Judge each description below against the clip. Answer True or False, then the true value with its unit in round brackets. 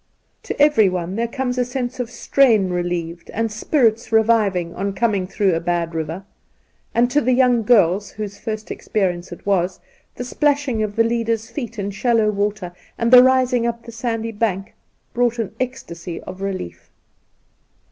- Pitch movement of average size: True (4.3 semitones)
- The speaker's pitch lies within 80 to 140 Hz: False (220 Hz)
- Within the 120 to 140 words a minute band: False (165 wpm)